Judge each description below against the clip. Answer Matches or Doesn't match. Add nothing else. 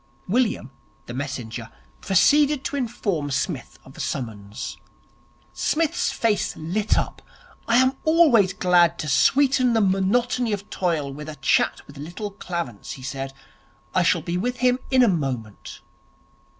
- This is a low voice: Doesn't match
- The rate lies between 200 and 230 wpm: Doesn't match